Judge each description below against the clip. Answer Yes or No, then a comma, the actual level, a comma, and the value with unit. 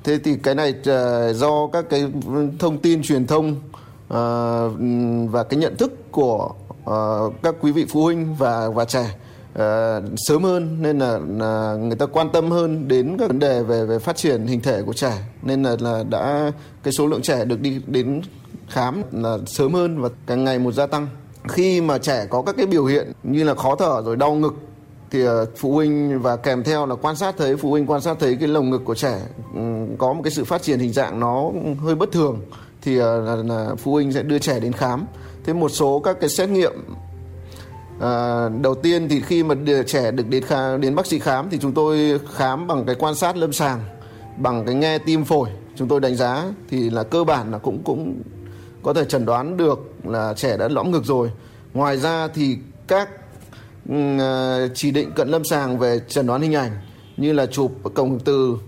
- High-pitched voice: No, low, 135 Hz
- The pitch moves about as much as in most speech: Yes, average, 4.1 semitones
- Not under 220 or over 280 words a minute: No, average, 205 wpm